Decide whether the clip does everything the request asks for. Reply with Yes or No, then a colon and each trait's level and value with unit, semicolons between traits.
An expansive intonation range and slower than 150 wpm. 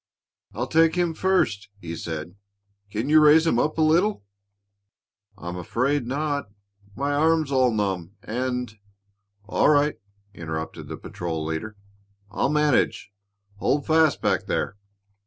Yes: wide, 7.2 semitones; slow, 135 wpm